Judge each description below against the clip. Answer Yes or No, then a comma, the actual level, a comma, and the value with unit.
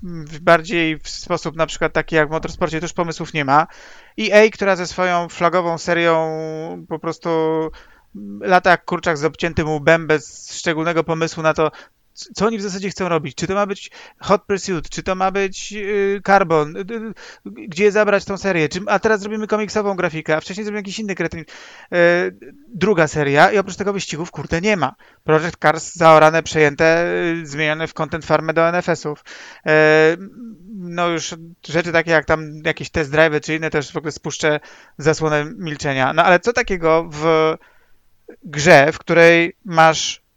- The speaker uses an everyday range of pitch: Yes, average, 3.3 semitones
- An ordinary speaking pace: No, fast, 170 wpm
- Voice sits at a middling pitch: Yes, medium, 165 Hz